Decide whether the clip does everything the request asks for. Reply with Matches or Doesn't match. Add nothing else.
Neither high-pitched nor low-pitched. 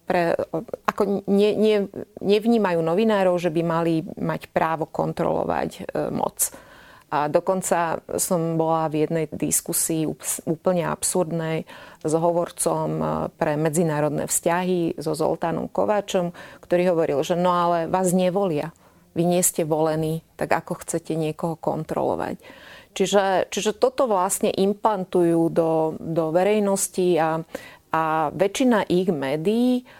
Matches